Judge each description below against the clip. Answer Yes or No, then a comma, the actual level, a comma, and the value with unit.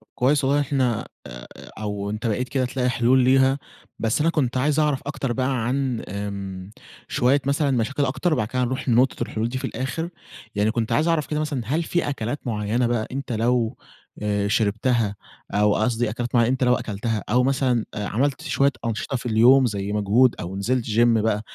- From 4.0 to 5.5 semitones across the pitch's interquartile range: No, average, 3.6 semitones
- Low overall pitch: Yes, low, 125 Hz